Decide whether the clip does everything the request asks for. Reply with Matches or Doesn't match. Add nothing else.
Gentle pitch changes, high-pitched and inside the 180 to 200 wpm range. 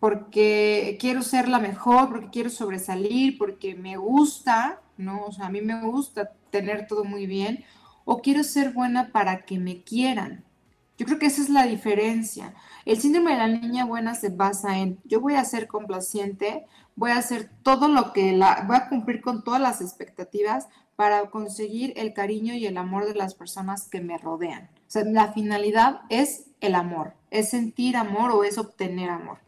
Doesn't match